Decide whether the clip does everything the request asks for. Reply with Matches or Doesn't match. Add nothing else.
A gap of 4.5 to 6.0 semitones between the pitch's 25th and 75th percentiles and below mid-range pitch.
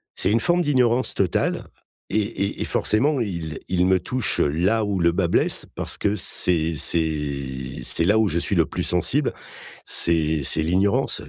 Matches